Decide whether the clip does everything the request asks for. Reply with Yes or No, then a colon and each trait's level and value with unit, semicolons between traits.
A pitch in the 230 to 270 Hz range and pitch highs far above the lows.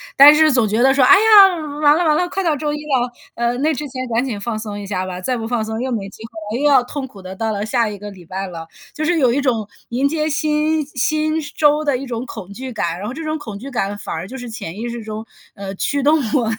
Yes: high, 245 Hz; wide, 5.7 semitones